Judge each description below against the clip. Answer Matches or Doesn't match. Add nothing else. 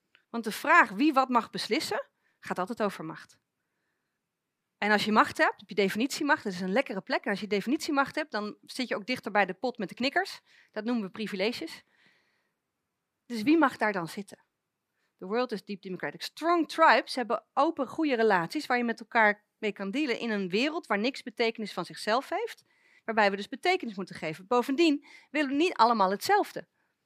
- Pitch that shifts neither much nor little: Doesn't match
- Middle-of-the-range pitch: Doesn't match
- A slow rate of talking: Doesn't match